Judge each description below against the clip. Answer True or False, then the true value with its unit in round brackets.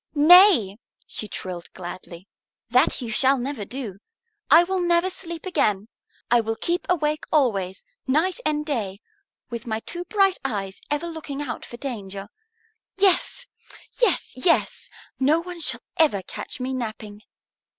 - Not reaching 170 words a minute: True (140 wpm)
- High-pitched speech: True (265 Hz)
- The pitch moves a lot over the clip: True (7.8 semitones)